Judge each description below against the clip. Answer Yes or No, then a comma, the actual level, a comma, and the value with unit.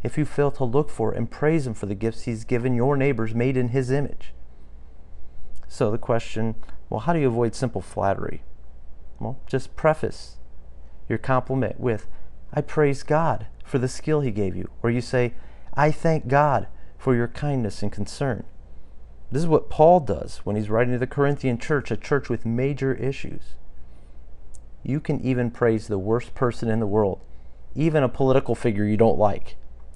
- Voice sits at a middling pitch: No, low, 120 Hz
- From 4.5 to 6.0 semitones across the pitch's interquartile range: Yes, average, 4.8 semitones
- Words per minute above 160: Yes, average, 180 wpm